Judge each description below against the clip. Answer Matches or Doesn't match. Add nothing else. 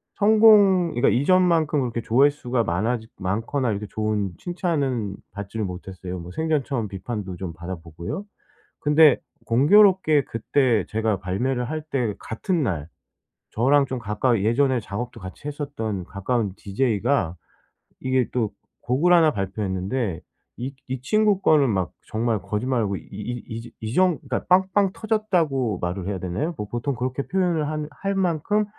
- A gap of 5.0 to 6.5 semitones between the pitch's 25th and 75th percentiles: Doesn't match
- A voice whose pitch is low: Matches